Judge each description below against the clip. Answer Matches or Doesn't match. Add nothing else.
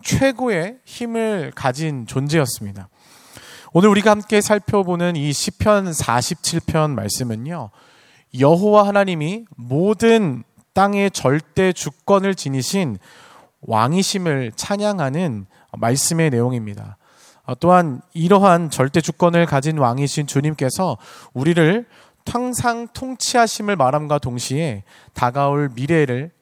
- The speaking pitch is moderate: Matches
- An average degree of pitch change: Doesn't match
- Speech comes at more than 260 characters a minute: Doesn't match